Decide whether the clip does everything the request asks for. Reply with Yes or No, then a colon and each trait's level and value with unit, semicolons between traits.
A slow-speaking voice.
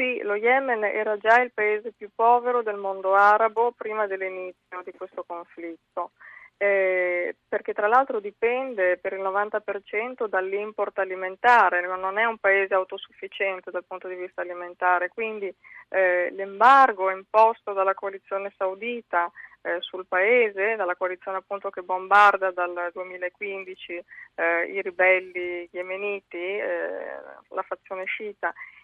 No: average, 130 wpm